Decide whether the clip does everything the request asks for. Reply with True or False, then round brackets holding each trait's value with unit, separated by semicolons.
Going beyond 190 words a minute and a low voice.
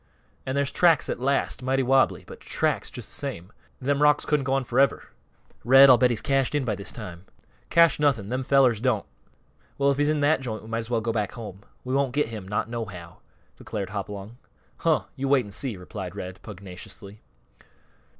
True (200 wpm; 125 Hz)